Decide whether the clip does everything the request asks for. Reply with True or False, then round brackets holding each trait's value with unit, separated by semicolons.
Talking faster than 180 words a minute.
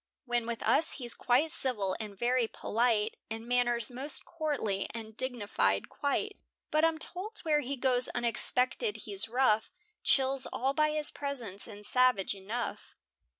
False (150 wpm)